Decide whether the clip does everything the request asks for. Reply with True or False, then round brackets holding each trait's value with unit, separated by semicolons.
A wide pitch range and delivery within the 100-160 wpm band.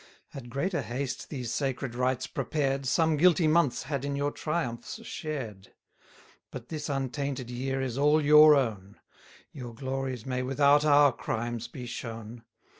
False (3.1 semitones; 145 wpm)